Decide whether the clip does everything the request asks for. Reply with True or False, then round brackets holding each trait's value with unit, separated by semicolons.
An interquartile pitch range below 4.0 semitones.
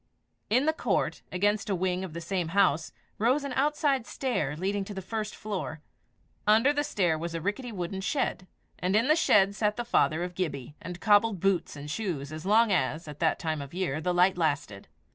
False (4.7 semitones)